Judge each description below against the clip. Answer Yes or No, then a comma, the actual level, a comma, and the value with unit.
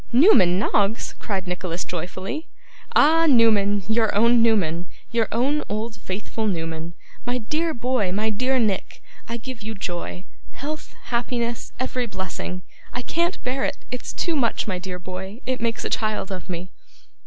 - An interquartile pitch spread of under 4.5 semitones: No, average, 4.8 semitones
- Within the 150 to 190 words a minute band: Yes, average, 155 wpm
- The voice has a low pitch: No, high, 220 Hz